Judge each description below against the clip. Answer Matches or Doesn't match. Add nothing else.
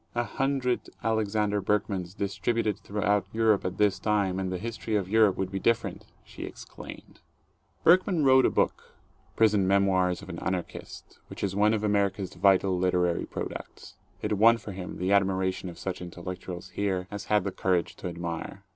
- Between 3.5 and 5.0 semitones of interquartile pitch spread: Doesn't match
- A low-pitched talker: Matches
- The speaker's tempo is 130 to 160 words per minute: Doesn't match